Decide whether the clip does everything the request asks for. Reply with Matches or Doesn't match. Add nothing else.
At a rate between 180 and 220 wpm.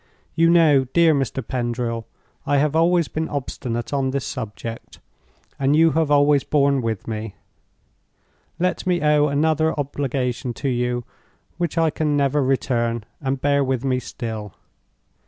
Doesn't match